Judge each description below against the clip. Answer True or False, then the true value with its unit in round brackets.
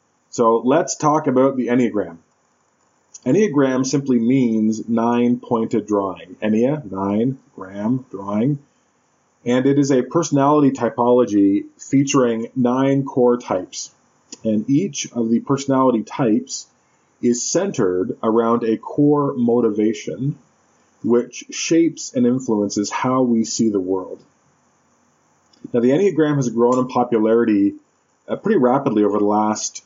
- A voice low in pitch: True (120 Hz)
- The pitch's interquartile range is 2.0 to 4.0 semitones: True (3.6 semitones)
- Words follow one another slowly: True (120 wpm)